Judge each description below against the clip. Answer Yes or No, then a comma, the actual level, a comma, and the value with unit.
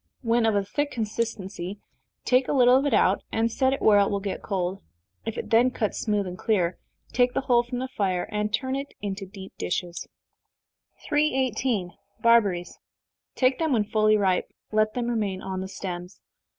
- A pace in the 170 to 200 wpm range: Yes, average, 185 wpm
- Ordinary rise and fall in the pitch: Yes, average, 4.3 semitones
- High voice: Yes, high, 215 Hz